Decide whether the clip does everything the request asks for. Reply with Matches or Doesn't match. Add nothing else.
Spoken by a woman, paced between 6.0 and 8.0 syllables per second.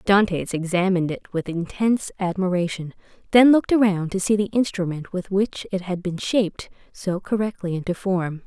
Doesn't match